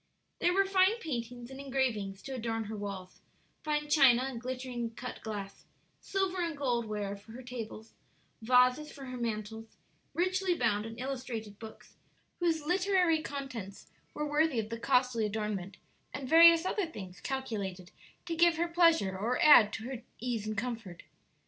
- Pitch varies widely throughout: Yes, wide, 5.7 semitones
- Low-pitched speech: No, very high, 250 Hz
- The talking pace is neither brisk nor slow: Yes, average, 160 wpm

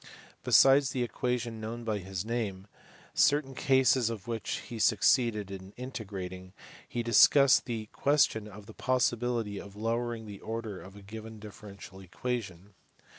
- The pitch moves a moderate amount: Yes, average, 3.3 semitones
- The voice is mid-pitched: No, low, 110 Hz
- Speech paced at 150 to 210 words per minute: No, average, 140 wpm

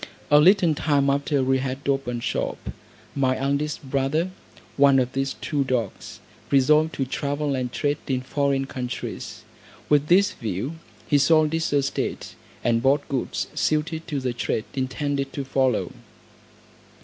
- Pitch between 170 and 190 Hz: No, medium, 140 Hz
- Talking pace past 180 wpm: No, average, 145 wpm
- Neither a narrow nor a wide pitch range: No, narrow, 2.2 semitones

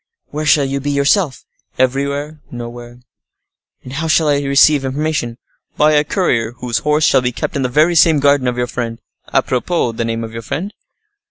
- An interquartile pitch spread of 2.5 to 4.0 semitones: Yes, average, 3.7 semitones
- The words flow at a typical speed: Yes, average, 190 wpm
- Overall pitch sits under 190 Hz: Yes, medium, 140 Hz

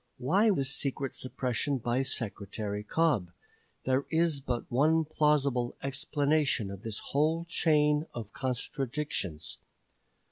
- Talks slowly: Yes, slow, 110 wpm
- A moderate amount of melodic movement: Yes, average, 4.0 semitones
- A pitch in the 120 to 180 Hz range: Yes, low, 135 Hz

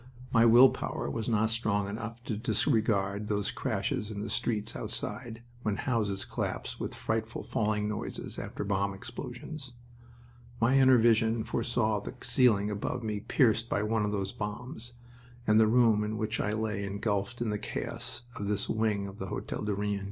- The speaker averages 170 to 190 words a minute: Yes, average, 175 wpm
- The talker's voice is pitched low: Yes, low, 110 Hz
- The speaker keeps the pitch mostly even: Yes, narrow, 2.2 semitones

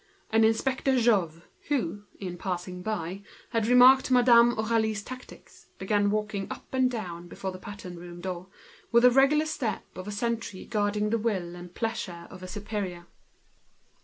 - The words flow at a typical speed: Yes, average, 160 wpm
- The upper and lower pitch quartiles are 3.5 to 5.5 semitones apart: Yes, average, 4.2 semitones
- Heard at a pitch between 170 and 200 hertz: No, high, 210 Hz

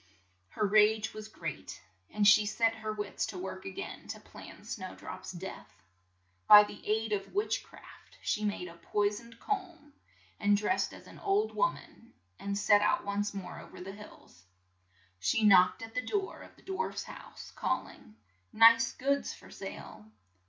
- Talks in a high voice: Yes, high, 210 Hz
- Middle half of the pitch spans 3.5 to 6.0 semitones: No, narrow, 2.4 semitones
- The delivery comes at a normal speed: Yes, average, 180 wpm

